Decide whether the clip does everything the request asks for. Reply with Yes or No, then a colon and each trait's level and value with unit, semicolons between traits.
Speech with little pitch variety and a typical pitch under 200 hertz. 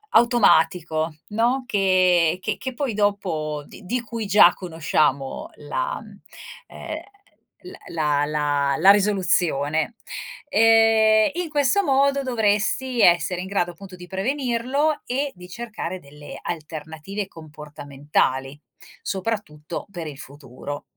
No: wide, 7.0 semitones; medium, 185 Hz